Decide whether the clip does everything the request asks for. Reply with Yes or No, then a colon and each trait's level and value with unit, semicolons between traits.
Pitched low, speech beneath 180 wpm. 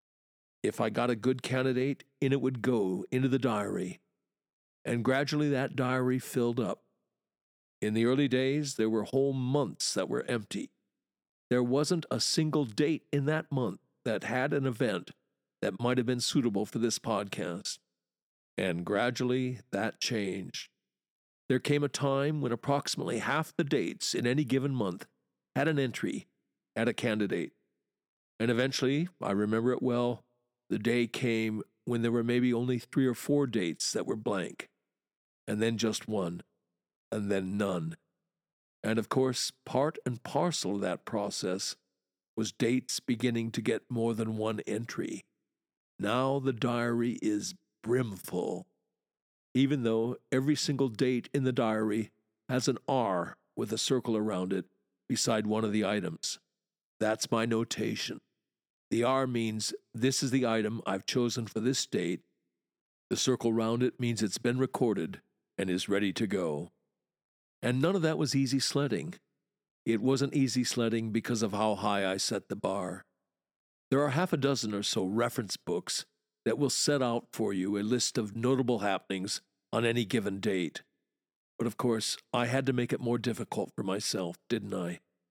Yes: low, 120 Hz; average, 160 wpm